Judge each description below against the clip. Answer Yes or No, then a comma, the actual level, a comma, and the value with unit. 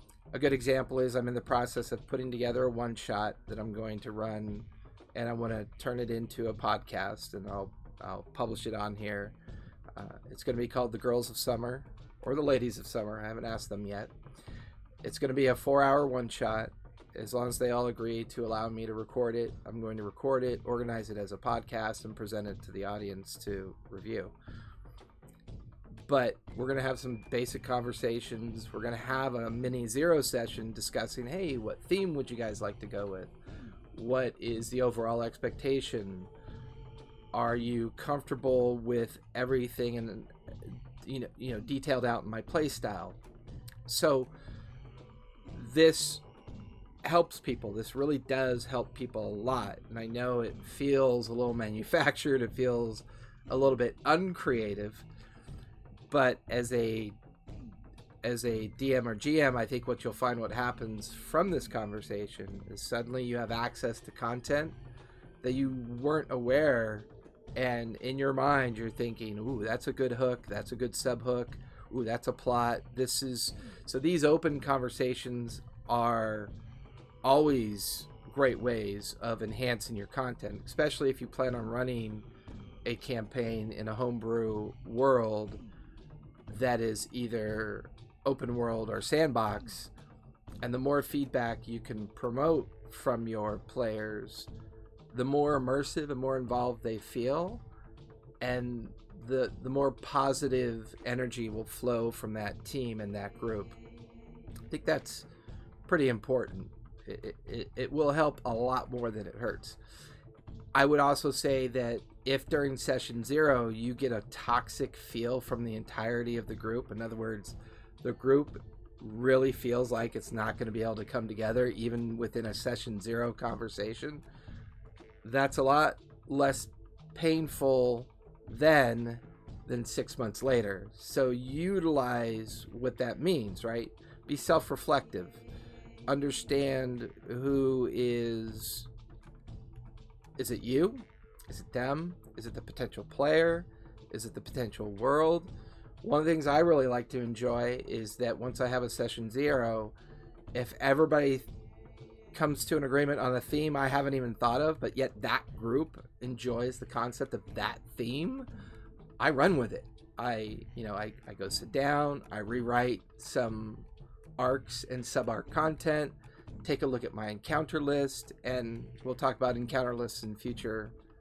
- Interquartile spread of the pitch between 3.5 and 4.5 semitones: No, average, 2.8 semitones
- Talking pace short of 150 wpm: No, average, 155 wpm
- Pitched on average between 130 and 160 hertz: No, low, 120 Hz